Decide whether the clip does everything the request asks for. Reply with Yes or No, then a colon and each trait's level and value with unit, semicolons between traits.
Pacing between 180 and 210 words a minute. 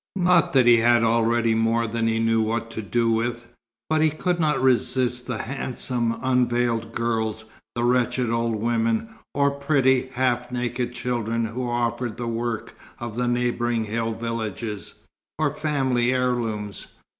No: average, 155 wpm